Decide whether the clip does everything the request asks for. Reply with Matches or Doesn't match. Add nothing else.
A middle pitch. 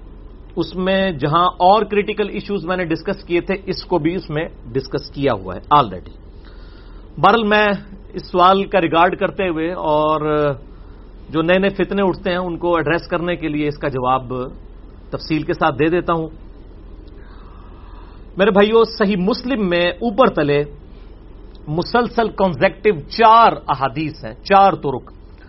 Matches